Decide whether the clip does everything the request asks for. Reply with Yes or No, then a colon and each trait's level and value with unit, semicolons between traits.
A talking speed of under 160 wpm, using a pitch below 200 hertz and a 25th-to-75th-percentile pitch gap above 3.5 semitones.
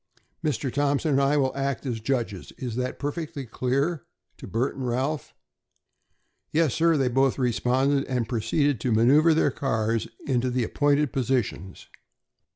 No: average, 150 wpm; low, 135 Hz; average, 2.9 semitones